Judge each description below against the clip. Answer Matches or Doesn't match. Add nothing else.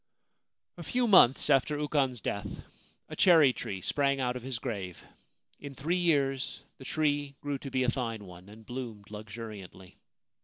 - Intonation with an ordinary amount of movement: Matches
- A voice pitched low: Matches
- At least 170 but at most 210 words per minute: Doesn't match